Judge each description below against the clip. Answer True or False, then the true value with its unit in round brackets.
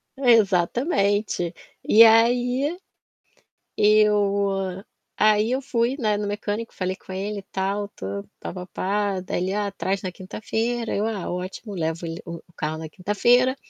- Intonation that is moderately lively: True (3.3 semitones)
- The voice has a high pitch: True (205 Hz)